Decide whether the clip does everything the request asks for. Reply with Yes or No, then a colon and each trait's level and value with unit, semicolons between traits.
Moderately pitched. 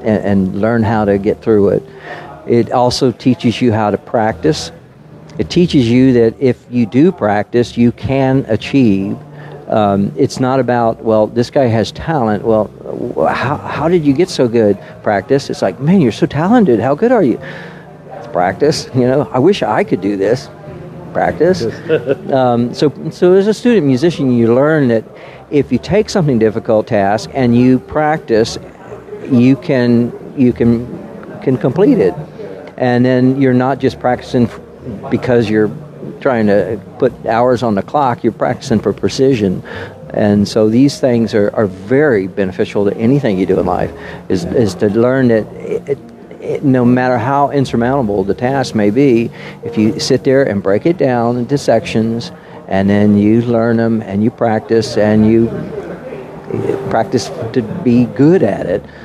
No: low, 120 Hz